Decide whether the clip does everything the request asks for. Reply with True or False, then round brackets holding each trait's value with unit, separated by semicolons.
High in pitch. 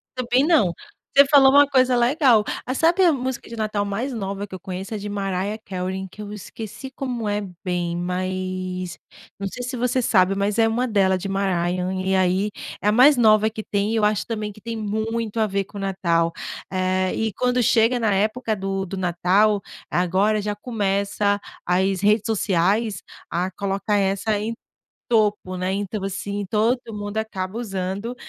True (205 Hz)